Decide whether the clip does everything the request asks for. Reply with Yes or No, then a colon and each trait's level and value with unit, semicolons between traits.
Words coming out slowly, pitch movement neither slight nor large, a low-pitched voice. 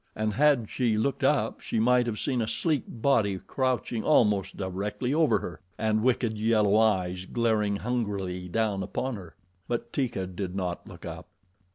No: average, 165 wpm; average, 3.8 semitones; low, 110 Hz